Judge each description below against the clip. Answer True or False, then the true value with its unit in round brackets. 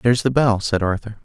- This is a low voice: True (110 Hz)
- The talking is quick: True (240 wpm)